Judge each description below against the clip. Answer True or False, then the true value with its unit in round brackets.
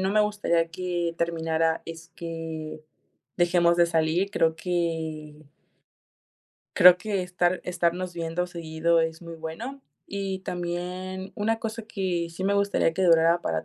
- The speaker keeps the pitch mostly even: True (2.3 semitones)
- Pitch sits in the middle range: True (175 Hz)